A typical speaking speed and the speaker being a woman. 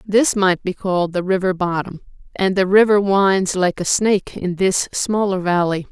Yes: average, 185 wpm; female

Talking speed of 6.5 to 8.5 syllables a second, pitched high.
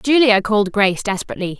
Yes: 7.1 syllables/s; high, 210 Hz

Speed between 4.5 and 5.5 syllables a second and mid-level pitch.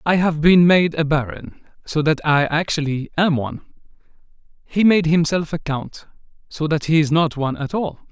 Yes: 5.0 syllables/s; medium, 160 Hz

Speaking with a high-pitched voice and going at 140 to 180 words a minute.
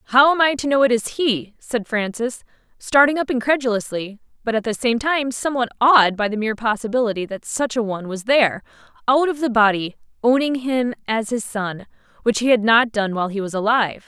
No: high, 235 Hz; fast, 205 wpm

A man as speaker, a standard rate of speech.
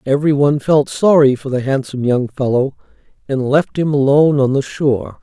Yes: male; average, 170 wpm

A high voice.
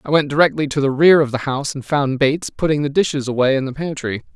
No: medium, 140 Hz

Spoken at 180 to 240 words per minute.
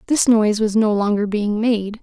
Yes: fast, 205 wpm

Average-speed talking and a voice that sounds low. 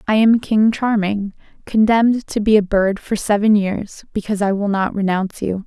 No: average, 190 wpm; high, 205 Hz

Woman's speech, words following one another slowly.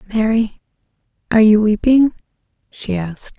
Yes: female; slow, 105 wpm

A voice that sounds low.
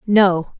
No: high, 190 Hz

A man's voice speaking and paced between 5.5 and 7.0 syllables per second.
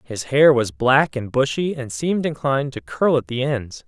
No: male; 4.8 syllables/s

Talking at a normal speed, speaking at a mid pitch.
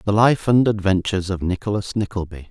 No: average, 165 wpm; low, 100 Hz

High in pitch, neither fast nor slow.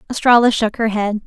Yes: high, 225 Hz; average, 190 wpm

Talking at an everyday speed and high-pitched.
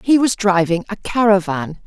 Yes: average, 160 wpm; high, 200 Hz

